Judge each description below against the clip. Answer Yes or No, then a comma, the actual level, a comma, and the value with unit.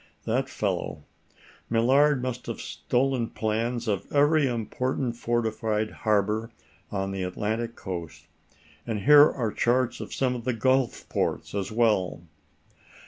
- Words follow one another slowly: Yes, slow, 130 wpm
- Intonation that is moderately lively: Yes, average, 3.1 semitones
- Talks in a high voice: No, low, 115 Hz